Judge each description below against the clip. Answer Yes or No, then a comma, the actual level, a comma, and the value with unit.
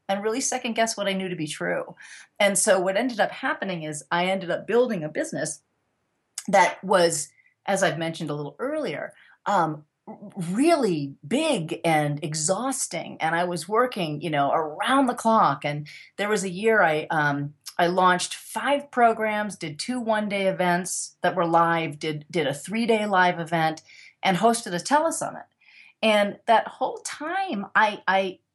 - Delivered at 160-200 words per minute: Yes, average, 170 wpm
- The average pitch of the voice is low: No, high, 190 Hz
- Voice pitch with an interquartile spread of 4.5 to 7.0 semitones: Yes, average, 5.2 semitones